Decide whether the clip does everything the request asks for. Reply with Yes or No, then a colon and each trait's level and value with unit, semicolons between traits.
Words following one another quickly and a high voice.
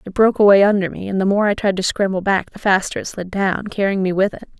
Yes: fast, 290 wpm; high, 195 Hz